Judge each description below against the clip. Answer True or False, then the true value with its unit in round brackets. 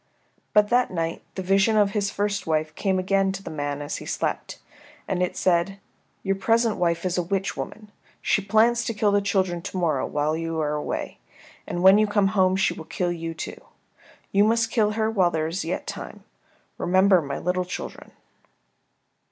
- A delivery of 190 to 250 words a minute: True (195 wpm)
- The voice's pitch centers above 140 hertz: True (190 Hz)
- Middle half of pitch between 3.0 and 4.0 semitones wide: True (3.4 semitones)